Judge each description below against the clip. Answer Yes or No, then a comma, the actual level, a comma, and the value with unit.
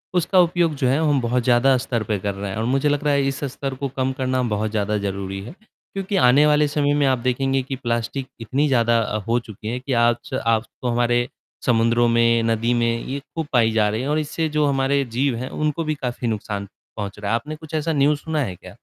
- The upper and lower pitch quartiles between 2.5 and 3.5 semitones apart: No, average, 3.9 semitones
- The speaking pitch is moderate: No, low, 130 Hz